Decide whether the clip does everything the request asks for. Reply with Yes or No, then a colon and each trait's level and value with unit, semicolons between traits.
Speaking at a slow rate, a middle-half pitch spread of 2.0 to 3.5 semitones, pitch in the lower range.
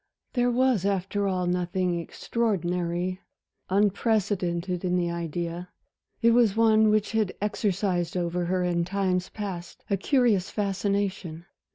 No: slow, 125 wpm; average, 2.9 semitones; medium, 185 Hz